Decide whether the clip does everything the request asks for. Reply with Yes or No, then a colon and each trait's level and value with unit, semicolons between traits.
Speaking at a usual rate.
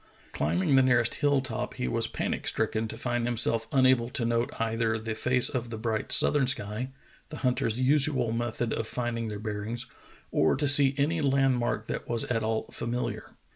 Yes: average, 185 wpm